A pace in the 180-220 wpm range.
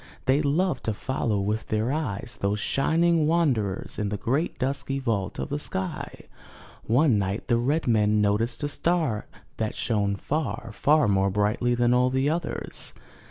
No: average, 160 wpm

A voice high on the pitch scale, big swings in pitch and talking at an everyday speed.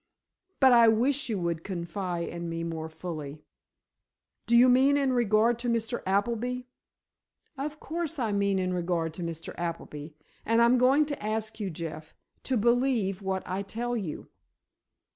Yes: high, 215 Hz; wide, 6.1 semitones; average, 160 wpm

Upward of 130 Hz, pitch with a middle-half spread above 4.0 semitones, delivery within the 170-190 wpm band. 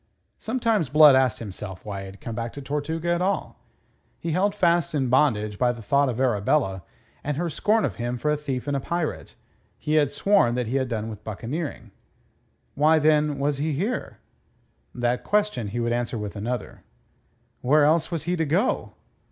Yes: medium, 140 Hz; average, 5.2 semitones; average, 185 wpm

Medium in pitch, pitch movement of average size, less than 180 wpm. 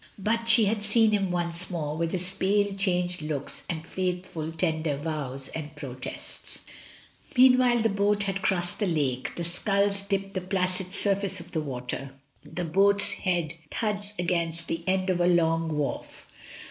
Yes: medium, 180 Hz; average, 3.6 semitones; average, 165 wpm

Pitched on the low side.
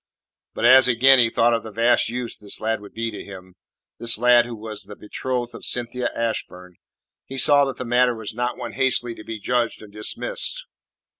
Yes: low, 120 Hz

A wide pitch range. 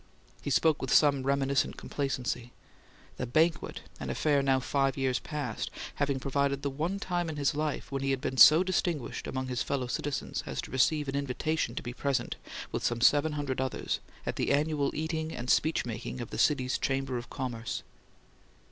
No: narrow, 2.5 semitones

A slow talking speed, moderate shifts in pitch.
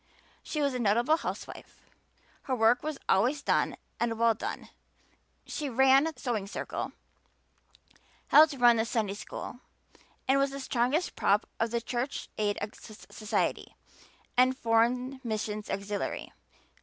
Yes: slow, 130 wpm; average, 3.3 semitones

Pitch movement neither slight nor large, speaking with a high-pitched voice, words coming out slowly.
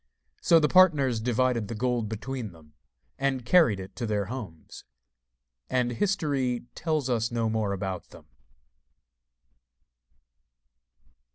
No: average, 3.8 semitones; low, 120 Hz; slow, 115 wpm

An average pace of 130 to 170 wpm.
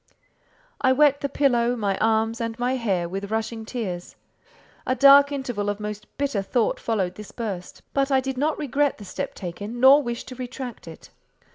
No: average, 180 wpm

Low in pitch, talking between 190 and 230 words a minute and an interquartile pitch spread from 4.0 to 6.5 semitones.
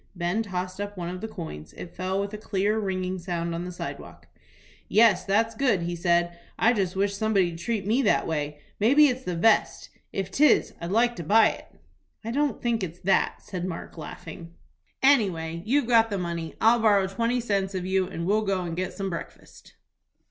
No: high, 190 Hz; average, 200 wpm; average, 4.3 semitones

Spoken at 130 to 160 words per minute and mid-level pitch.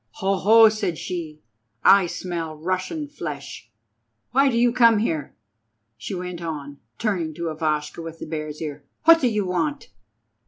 Yes: average, 155 wpm; medium, 175 Hz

